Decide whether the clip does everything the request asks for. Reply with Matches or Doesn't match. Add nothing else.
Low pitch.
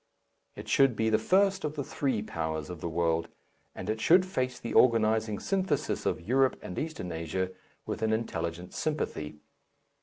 Matches